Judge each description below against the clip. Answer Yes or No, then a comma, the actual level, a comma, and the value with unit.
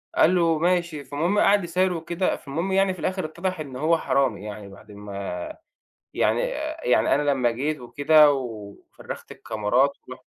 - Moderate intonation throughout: No, wide, 5.8 semitones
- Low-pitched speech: No, medium, 150 Hz